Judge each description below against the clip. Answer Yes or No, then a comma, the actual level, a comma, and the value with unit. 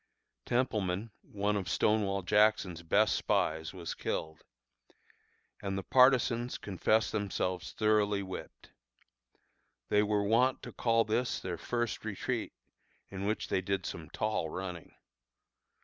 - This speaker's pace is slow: Yes, slow, 120 wpm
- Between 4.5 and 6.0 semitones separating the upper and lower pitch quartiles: No, average, 3.0 semitones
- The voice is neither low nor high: No, low, 100 Hz